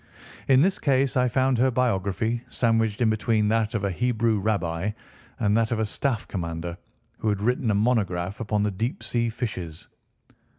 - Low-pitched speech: Yes, low, 110 Hz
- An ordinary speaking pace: Yes, average, 175 wpm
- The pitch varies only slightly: No, average, 3.2 semitones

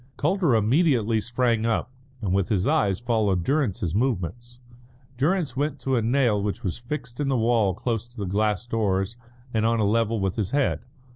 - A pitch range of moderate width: Yes, average, 3.6 semitones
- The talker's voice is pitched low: Yes, low, 115 Hz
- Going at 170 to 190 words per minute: Yes, average, 185 wpm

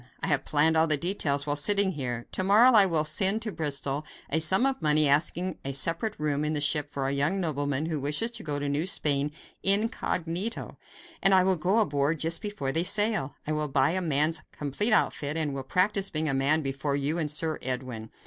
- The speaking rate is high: Yes, fast, 215 wpm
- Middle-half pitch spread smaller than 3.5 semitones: No, average, 4.7 semitones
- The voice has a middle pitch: Yes, medium, 155 Hz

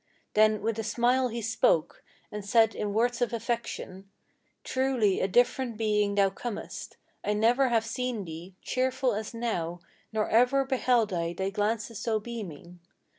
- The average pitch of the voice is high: Yes, high, 220 Hz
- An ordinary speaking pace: Yes, average, 155 wpm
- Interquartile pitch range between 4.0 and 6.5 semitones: No, average, 3.1 semitones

